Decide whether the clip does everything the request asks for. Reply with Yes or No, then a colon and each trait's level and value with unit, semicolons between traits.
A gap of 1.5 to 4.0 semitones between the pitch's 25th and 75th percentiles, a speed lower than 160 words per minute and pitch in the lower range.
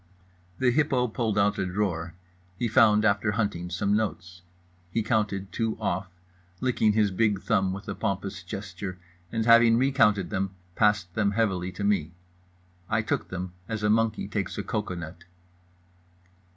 Yes: average, 2.9 semitones; average, 150 wpm; low, 105 Hz